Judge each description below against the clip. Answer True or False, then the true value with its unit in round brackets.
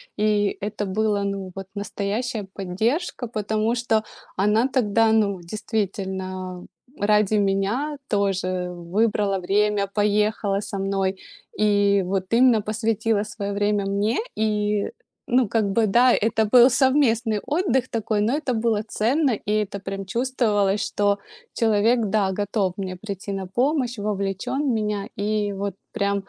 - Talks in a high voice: True (210 Hz)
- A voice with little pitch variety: True (2.3 semitones)